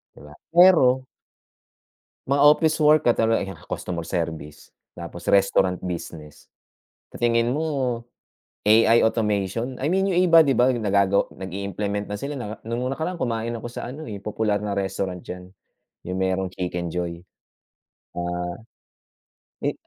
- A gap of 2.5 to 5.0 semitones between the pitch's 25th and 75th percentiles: No, wide, 5.5 semitones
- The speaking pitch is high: No, low, 105 Hz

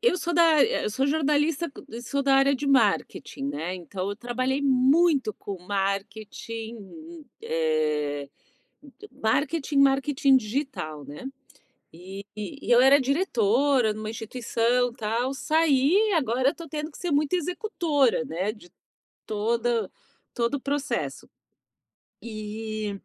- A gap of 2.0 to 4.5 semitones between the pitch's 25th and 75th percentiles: No, average, 5.3 semitones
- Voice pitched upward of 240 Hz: Yes, very high, 250 Hz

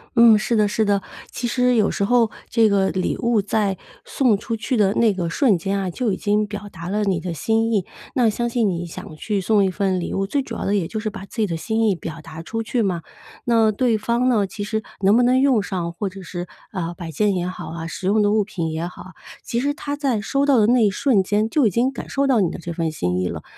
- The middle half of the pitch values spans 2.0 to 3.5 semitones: No, average, 3.9 semitones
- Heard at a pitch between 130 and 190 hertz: No, high, 205 Hz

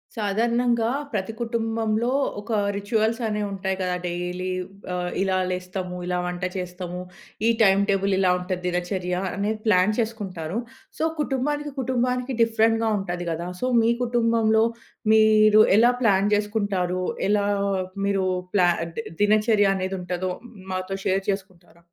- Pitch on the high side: Yes, high, 200 Hz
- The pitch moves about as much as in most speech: Yes, average, 3.5 semitones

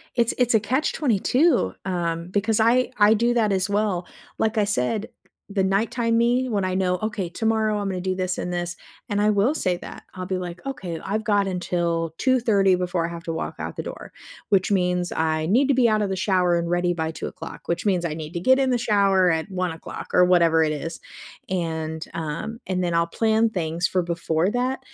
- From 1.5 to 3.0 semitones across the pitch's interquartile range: No, average, 4.2 semitones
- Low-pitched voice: No, high, 190 Hz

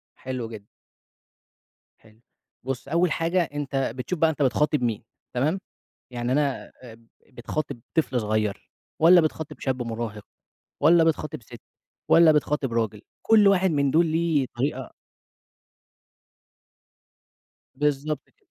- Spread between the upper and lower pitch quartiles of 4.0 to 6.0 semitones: Yes, average, 4.9 semitones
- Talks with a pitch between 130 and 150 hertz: Yes, medium, 140 Hz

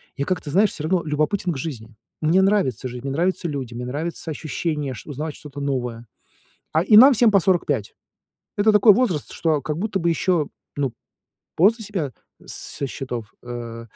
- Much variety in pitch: Yes, wide, 5.9 semitones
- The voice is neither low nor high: Yes, medium, 155 Hz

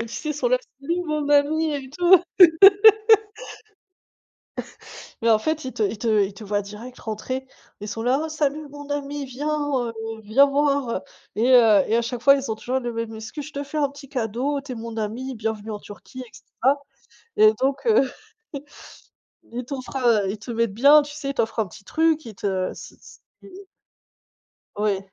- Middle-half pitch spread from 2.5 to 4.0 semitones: No, average, 4.6 semitones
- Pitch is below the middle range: No, very high, 260 Hz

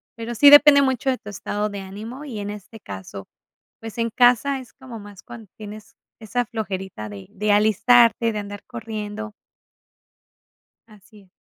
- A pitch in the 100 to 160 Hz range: No, high, 215 Hz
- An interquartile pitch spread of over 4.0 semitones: No, average, 2.8 semitones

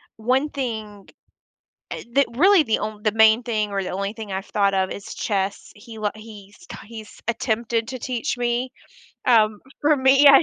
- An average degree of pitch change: Yes, average, 3.2 semitones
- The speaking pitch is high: Yes, high, 220 Hz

